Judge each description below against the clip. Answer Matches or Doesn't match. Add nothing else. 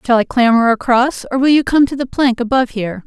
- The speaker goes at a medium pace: Doesn't match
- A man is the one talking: Doesn't match